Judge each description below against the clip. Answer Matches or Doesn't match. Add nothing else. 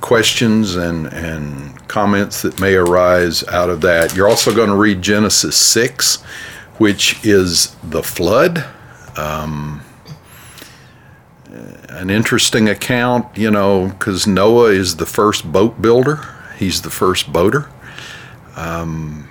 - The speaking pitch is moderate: Doesn't match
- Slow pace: Matches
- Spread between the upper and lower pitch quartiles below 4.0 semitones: Doesn't match